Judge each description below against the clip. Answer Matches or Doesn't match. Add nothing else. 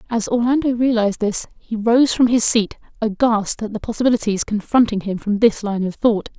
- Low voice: Doesn't match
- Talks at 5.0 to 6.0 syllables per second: Matches